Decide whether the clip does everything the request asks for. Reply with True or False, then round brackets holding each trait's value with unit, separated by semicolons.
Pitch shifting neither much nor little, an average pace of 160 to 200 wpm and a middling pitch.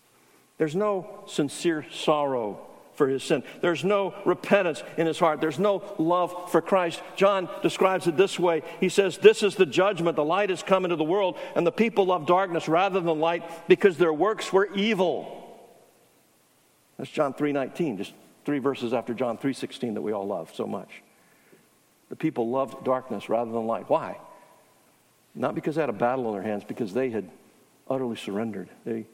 False (5.9 semitones; 180 wpm; 165 Hz)